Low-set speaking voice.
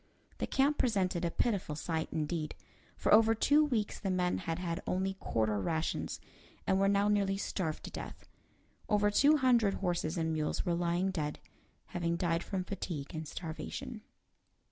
No: medium, 185 Hz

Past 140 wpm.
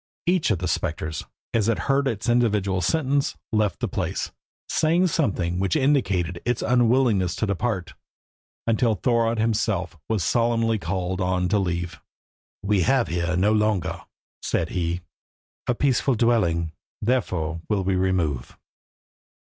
No: slow, 135 wpm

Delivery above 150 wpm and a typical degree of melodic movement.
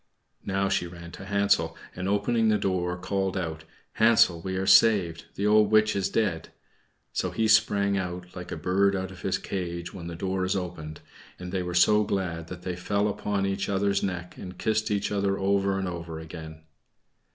No: average, 195 wpm; narrow, 2.3 semitones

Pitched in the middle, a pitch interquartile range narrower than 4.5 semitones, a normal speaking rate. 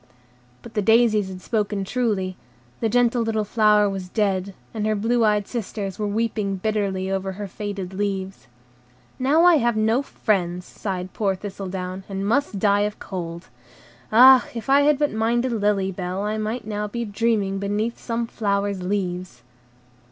No: high, 205 Hz; average, 2.8 semitones; average, 160 wpm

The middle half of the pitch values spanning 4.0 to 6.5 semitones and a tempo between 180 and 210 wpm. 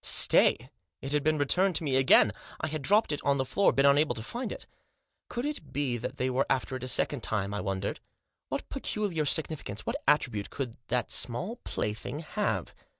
Yes: average, 4.4 semitones; average, 200 wpm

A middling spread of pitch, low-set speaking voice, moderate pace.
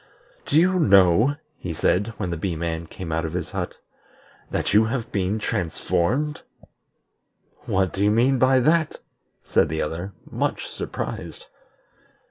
No: wide, 7.1 semitones; low, 100 Hz; average, 145 wpm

